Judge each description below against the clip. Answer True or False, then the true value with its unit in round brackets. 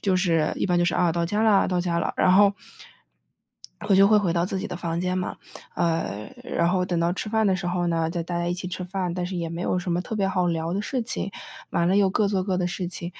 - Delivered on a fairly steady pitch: True (2.0 semitones)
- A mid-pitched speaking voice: True (180 Hz)